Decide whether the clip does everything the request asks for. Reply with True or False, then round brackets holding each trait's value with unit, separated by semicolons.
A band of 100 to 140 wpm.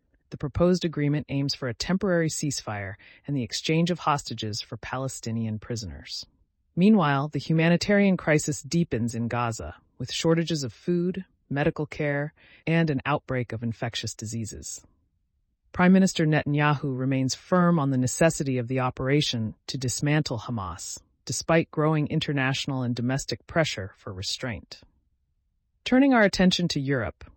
True (135 wpm)